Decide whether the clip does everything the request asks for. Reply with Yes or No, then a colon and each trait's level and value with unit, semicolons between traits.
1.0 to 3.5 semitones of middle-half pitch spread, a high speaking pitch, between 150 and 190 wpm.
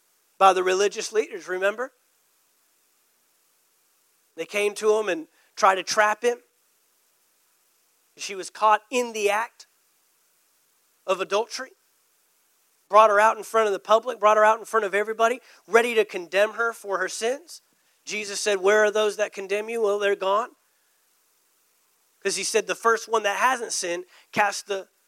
Yes: narrow, 2.4 semitones; high, 210 Hz; average, 160 wpm